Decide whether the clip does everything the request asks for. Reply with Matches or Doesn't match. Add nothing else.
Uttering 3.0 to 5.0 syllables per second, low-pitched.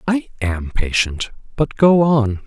Matches